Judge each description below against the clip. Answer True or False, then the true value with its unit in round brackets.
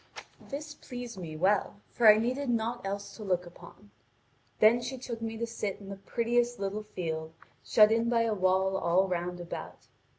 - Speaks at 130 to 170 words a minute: False (190 wpm)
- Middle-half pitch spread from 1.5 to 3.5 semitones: False (4.0 semitones)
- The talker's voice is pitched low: False (210 Hz)